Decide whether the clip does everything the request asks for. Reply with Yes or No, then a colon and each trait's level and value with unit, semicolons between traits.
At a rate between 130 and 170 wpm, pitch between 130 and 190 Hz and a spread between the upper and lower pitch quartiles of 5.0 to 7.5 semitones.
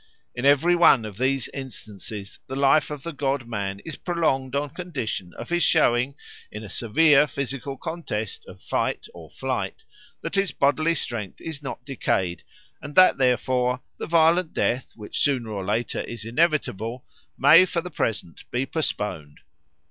Yes: average, 160 wpm; low, 135 Hz; wide, 5.6 semitones